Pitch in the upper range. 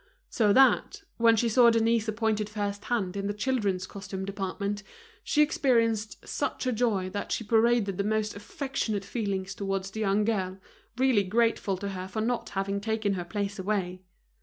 Yes: high, 210 Hz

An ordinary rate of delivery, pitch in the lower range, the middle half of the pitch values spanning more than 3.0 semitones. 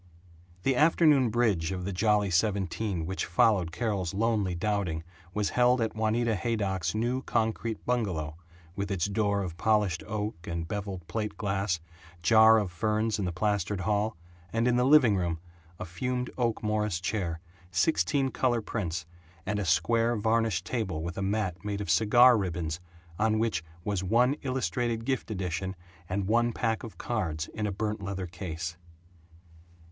Yes: average, 160 wpm; low, 105 Hz; average, 3.8 semitones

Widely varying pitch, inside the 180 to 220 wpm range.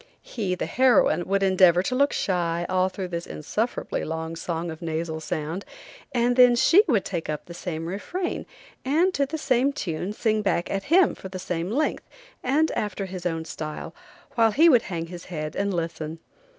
Yes: wide, 6.5 semitones; average, 190 wpm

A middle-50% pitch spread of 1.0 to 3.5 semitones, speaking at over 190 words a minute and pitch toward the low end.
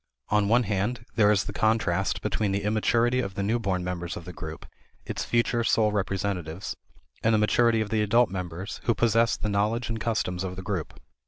Yes: average, 3.1 semitones; average, 200 wpm; low, 105 Hz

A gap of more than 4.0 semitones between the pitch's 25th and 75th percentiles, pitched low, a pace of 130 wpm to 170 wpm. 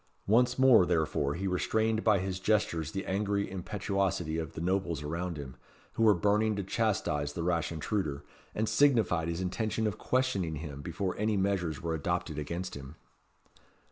Yes: average, 4.4 semitones; very low, 95 Hz; average, 165 wpm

